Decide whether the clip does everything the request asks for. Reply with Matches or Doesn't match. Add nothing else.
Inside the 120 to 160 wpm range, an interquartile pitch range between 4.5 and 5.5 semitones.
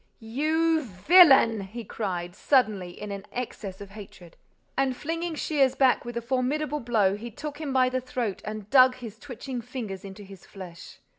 Doesn't match